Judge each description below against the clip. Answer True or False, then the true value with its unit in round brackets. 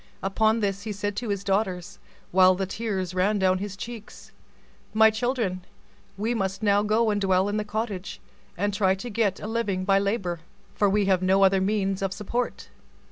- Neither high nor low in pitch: False (200 Hz)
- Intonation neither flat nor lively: False (2.1 semitones)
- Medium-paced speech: True (190 wpm)